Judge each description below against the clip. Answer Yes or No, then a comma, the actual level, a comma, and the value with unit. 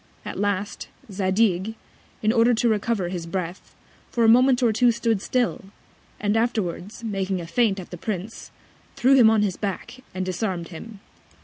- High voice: Yes, high, 210 Hz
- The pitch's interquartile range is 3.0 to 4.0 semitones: Yes, average, 3.5 semitones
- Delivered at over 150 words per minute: Yes, average, 170 wpm